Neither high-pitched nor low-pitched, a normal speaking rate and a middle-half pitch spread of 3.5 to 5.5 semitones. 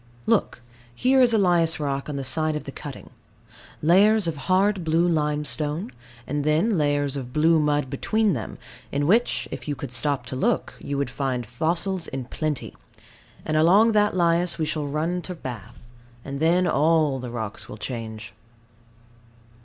Yes: medium, 150 Hz; average, 165 wpm; average, 4.0 semitones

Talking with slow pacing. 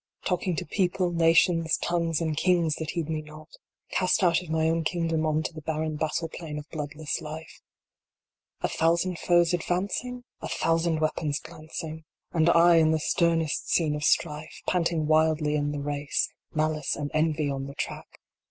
No: average, 175 wpm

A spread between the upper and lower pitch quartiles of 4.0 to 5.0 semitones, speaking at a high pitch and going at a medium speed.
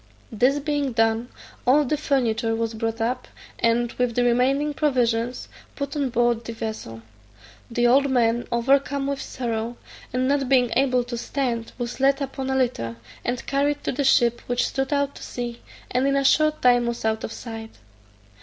No: average, 2.8 semitones; high, 245 Hz; average, 180 wpm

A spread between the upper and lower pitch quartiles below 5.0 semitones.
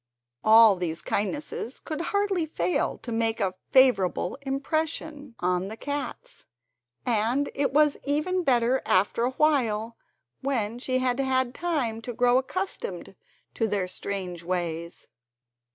No: wide, 5.5 semitones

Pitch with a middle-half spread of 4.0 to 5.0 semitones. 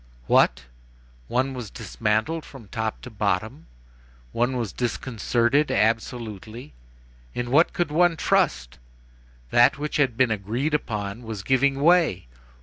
Yes: average, 4.4 semitones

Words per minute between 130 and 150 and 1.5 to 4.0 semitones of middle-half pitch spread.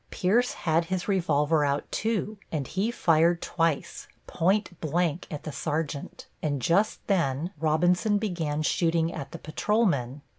Yes: average, 140 wpm; average, 3.7 semitones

